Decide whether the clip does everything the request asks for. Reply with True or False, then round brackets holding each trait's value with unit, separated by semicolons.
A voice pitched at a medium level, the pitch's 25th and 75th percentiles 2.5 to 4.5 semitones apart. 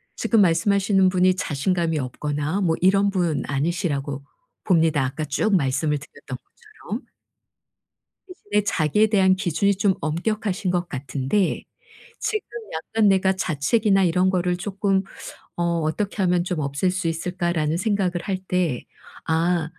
True (180 Hz; 3.8 semitones)